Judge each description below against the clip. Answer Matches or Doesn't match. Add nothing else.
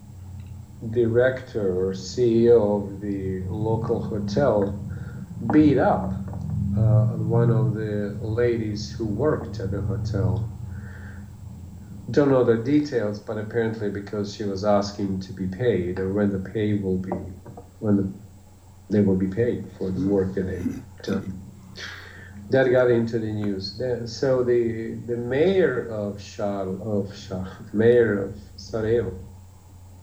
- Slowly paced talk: Matches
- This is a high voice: Doesn't match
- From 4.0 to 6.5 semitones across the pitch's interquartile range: Doesn't match